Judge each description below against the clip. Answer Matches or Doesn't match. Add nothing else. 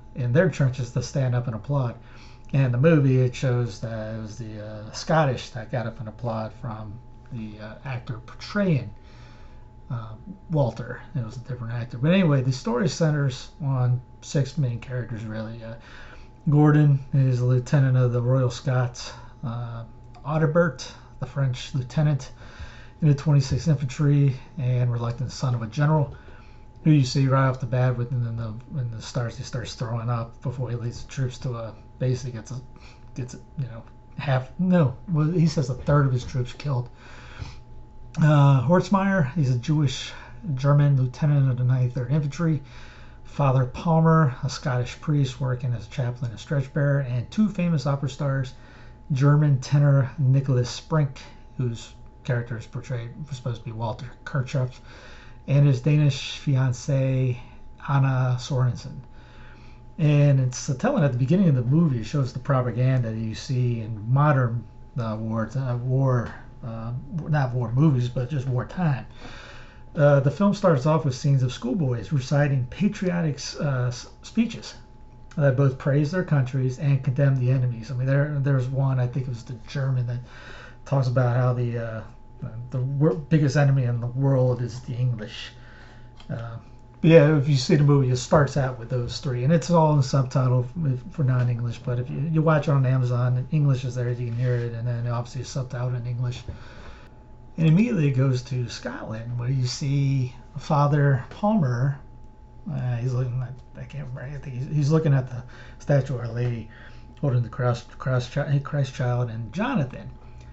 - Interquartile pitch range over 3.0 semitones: Doesn't match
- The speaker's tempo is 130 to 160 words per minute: Doesn't match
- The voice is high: Doesn't match